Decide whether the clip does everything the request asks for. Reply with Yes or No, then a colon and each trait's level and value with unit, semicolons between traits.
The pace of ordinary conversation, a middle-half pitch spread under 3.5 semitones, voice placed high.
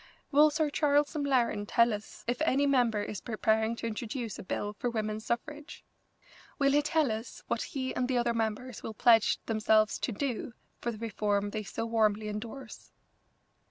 No: average, 175 wpm; average, 3.8 semitones; high, 230 Hz